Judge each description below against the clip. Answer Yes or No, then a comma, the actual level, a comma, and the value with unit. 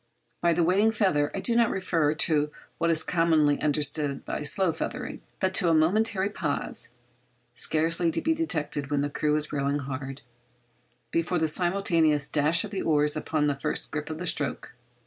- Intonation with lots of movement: No, average, 3.4 semitones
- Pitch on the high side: No, medium, 160 Hz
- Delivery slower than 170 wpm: No, average, 180 wpm